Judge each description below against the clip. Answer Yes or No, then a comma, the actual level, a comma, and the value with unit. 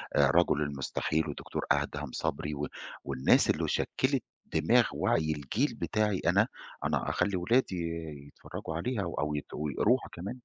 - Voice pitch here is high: No, very low, 80 Hz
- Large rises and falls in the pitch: Yes, wide, 5.8 semitones